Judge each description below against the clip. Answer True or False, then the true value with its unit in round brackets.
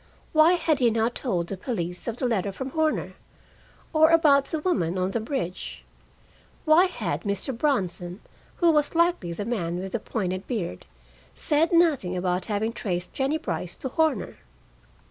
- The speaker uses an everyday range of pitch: False (8.8 semitones)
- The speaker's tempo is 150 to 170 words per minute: True (165 wpm)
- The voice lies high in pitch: True (230 Hz)